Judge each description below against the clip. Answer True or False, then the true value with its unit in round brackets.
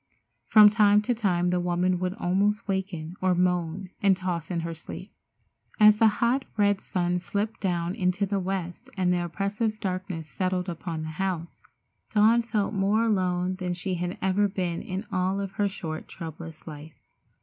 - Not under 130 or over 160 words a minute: False (170 wpm)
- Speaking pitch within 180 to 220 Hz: True (185 Hz)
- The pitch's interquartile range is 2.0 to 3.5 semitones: True (2.5 semitones)